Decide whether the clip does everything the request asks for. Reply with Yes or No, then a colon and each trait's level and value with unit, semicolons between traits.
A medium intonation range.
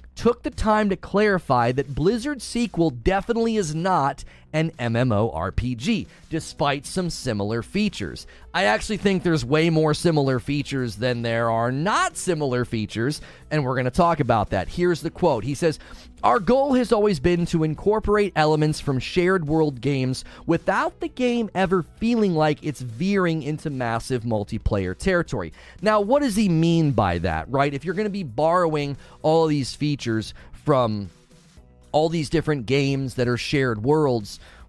No: wide, 6.9 semitones